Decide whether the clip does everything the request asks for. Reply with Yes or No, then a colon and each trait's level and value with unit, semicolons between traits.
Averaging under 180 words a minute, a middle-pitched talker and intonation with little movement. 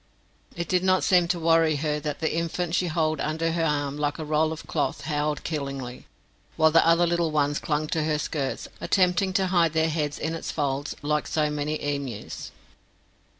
No: average, 195 wpm; medium, 155 Hz; narrow, 2.1 semitones